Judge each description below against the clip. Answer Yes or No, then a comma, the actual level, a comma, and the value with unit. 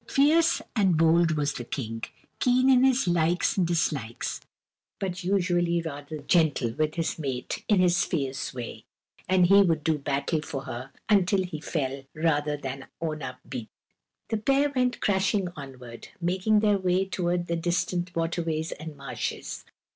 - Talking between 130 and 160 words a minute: Yes, average, 155 wpm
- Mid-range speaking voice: Yes, medium, 170 Hz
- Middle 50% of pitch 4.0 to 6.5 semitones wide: Yes, average, 4.5 semitones